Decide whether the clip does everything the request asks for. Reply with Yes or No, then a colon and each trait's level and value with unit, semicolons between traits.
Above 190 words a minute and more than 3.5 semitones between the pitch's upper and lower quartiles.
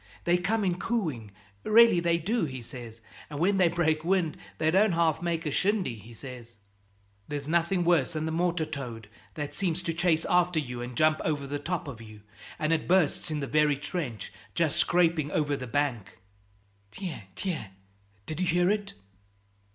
No: average, 180 wpm; average, 4.0 semitones